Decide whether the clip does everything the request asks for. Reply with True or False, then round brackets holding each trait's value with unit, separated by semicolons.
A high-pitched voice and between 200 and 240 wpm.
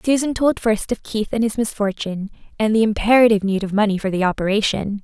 True (215 Hz; 205 wpm)